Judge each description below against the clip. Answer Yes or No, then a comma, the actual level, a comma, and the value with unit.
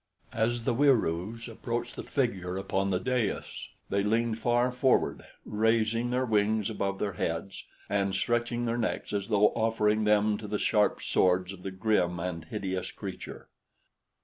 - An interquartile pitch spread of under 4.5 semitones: Yes, average, 3.1 semitones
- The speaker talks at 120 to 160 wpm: Yes, average, 155 wpm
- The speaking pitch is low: Yes, low, 105 Hz